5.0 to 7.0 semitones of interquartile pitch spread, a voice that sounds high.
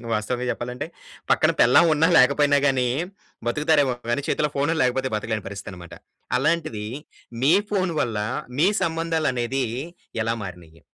No: wide, 5.5 semitones; low, 130 Hz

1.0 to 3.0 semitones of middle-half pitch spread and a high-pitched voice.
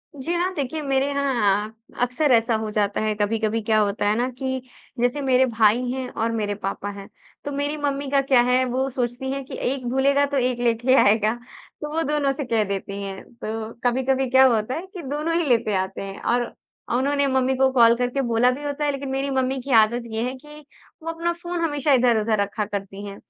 No: average, 4.0 semitones; very high, 255 Hz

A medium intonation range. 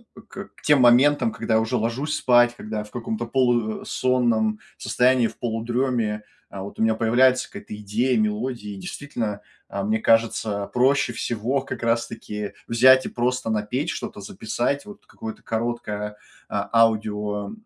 Yes: average, 3.1 semitones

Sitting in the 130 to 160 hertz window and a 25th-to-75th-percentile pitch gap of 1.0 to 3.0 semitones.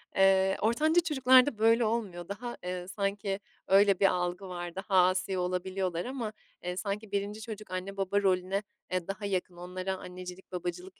No: high, 195 Hz; narrow, 2.5 semitones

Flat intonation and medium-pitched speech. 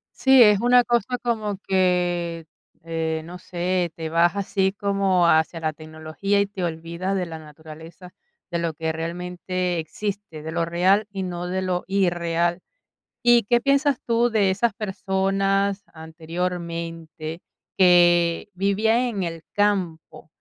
No: average, 3.1 semitones; medium, 180 Hz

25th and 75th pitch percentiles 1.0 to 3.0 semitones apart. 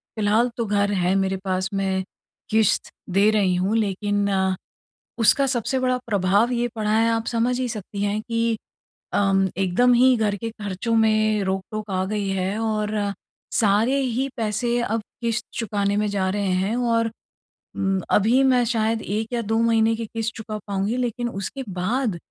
Yes: average, 2.7 semitones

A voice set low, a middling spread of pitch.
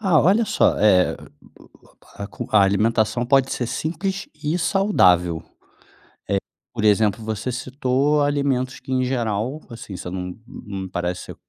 No: low, 120 Hz; wide, 6.1 semitones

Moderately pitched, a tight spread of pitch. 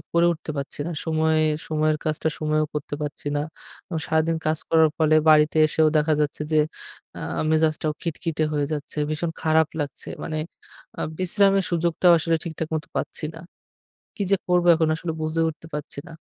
Yes: medium, 160 Hz; narrow, 1.3 semitones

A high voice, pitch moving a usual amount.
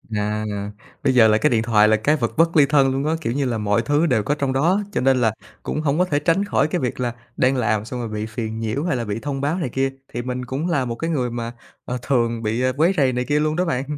No: low, 130 Hz; average, 4.3 semitones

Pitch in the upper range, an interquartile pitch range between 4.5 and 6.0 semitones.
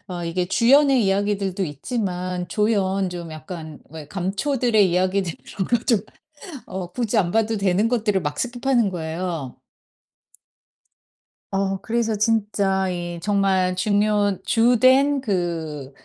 No: high, 195 Hz; average, 3.9 semitones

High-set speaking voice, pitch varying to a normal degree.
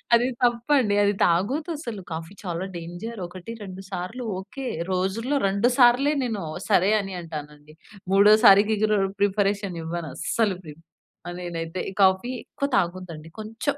Yes: high, 195 Hz; average, 4.7 semitones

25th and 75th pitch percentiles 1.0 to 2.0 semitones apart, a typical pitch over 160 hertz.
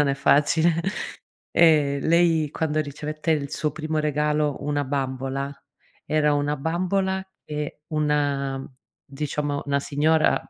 No: narrow, 1.7 semitones; medium, 150 Hz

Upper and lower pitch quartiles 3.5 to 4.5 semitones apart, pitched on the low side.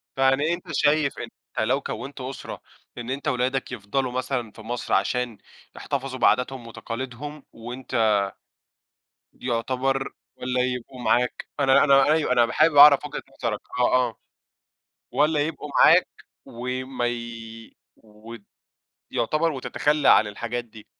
No: average, 2.8 semitones; low, 130 Hz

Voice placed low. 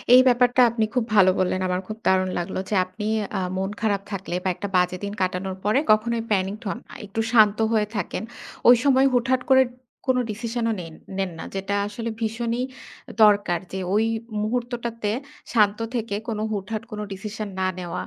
No: high, 210 Hz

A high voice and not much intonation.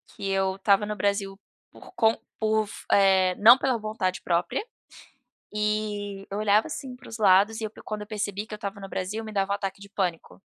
Yes: high, 205 Hz; narrow, 1.9 semitones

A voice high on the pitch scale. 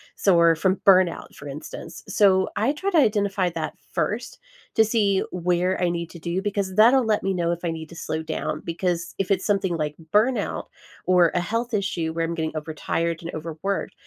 No: medium, 180 Hz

